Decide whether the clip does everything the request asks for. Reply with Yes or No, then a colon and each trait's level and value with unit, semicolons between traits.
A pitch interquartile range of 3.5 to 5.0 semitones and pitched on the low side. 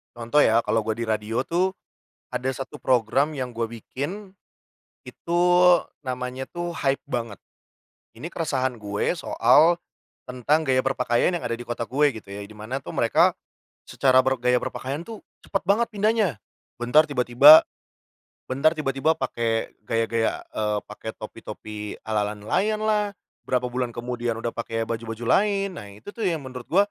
No: wide, 5.5 semitones; low, 125 Hz